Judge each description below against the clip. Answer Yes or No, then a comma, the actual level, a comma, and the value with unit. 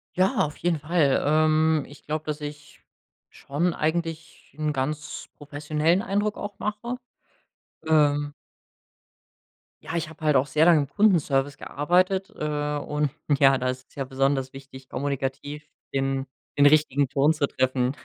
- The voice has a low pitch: No, medium, 150 Hz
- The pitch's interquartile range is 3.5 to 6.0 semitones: No, narrow, 2.5 semitones